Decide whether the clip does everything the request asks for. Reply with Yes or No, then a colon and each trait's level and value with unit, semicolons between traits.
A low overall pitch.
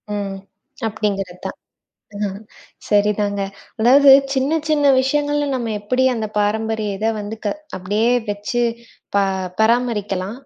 No: high, 215 Hz